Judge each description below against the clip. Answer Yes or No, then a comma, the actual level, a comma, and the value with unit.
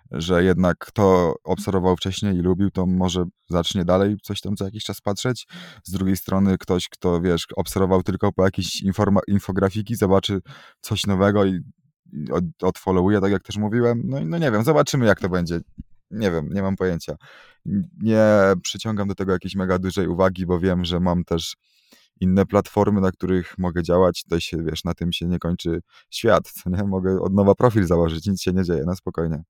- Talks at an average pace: No, fast, 185 wpm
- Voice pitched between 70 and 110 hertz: Yes, very low, 95 Hz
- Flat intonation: Yes, narrow, 2.1 semitones